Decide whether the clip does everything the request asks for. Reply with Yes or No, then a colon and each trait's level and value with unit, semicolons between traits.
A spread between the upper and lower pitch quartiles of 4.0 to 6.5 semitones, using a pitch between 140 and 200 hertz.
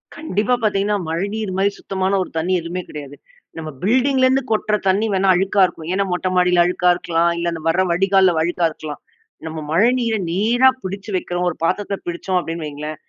No: average, 3.3 semitones; medium, 185 Hz